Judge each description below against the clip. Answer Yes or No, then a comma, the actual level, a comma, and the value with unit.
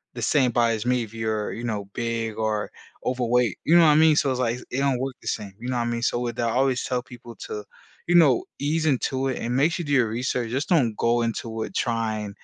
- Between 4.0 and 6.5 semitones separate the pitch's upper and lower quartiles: No, average, 2.8 semitones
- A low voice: Yes, low, 120 Hz